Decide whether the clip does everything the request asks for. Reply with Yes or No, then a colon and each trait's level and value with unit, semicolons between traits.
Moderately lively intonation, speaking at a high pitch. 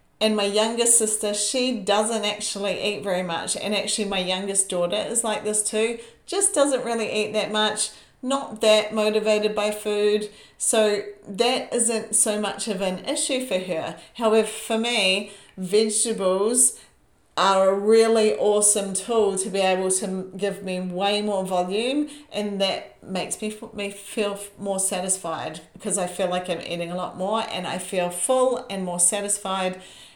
No: narrow, 2.3 semitones; high, 210 Hz